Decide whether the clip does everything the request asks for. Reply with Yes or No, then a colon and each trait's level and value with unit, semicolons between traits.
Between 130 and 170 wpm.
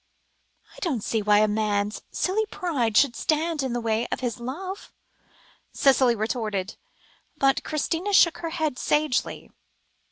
Yes: average, 140 wpm